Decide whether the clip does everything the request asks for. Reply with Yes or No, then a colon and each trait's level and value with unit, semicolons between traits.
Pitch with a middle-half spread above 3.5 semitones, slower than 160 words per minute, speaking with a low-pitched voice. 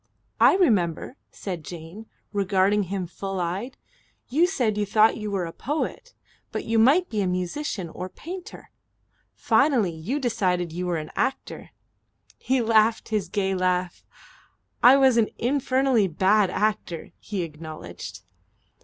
No: wide, 5.4 semitones; average, 140 wpm; high, 205 Hz